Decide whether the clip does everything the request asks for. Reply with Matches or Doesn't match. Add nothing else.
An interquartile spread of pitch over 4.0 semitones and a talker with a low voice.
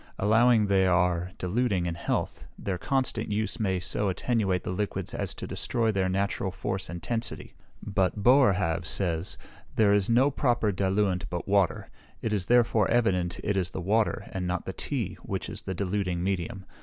Doesn't match